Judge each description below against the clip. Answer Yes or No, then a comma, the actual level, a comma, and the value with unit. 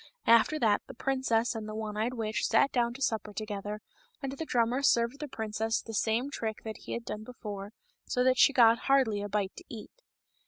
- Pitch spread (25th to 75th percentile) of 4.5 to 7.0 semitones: No, average, 3.0 semitones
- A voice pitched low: No, high, 225 Hz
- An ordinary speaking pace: No, fast, 210 wpm